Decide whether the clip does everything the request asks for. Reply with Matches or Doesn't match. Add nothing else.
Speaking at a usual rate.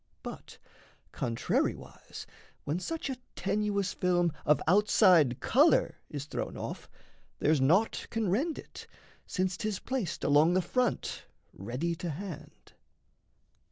Doesn't match